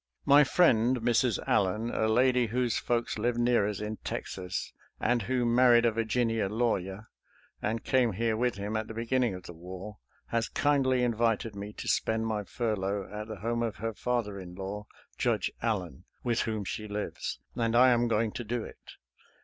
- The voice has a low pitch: Yes, low, 115 Hz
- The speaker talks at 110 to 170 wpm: No, average, 180 wpm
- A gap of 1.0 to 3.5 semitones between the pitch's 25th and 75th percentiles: Yes, narrow, 2.6 semitones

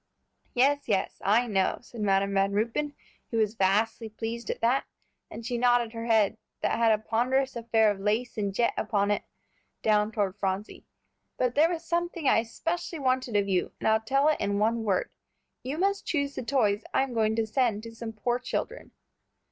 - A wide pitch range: No, average, 3.4 semitones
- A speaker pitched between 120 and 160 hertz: No, high, 230 Hz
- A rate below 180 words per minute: No, average, 190 wpm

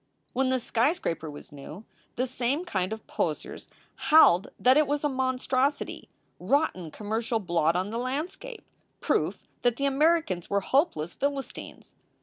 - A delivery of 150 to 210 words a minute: No, average, 140 wpm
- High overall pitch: Yes, very high, 255 Hz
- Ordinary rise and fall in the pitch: No, wide, 6.8 semitones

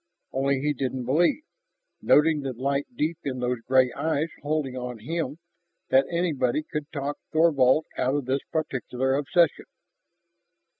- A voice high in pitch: No, medium, 140 Hz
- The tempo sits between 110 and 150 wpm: Yes, average, 140 wpm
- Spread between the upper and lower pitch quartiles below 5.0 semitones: Yes, average, 3.2 semitones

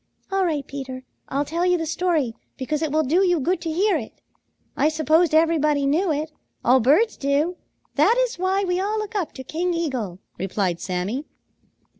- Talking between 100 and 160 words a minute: No, average, 185 wpm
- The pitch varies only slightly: No, average, 4.5 semitones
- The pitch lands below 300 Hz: No, very high, 315 Hz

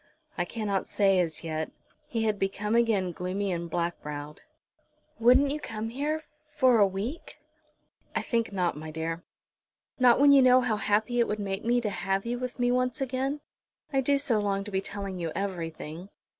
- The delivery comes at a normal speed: Yes, average, 185 wpm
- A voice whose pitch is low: No, high, 210 Hz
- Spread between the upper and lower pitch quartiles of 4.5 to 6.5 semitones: Yes, average, 5.2 semitones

